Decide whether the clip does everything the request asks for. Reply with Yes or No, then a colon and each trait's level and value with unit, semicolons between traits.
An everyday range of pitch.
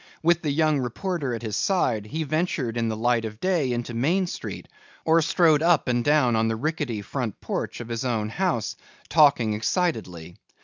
No: wide, 6.1 semitones